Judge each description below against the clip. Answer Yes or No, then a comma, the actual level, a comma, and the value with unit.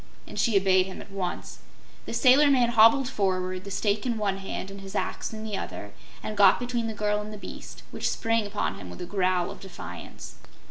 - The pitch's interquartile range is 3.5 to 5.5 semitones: No, average, 3.1 semitones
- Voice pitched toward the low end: No, high, 205 Hz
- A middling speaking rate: No, fast, 220 wpm